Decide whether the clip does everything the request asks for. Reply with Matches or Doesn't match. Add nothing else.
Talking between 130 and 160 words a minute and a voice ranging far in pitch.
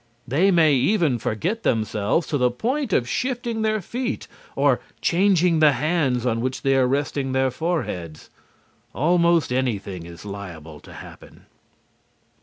Matches